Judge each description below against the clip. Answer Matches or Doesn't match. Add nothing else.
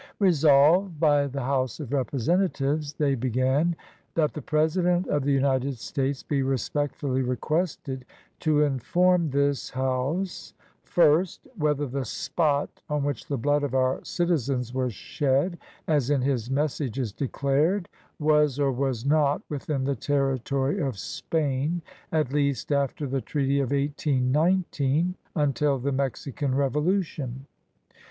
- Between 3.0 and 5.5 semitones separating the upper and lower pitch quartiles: Doesn't match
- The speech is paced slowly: Matches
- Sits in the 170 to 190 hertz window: Doesn't match